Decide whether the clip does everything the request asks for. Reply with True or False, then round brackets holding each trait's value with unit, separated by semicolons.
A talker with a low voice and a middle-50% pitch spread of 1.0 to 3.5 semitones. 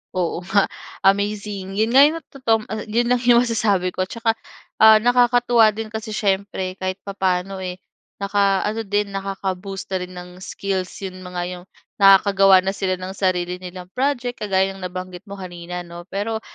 False (195 Hz; 2.8 semitones)